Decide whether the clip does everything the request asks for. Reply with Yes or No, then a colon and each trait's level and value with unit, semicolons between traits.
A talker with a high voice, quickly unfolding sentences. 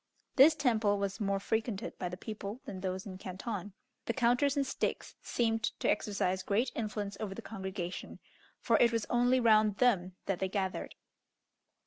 No: high, 210 Hz; average, 165 wpm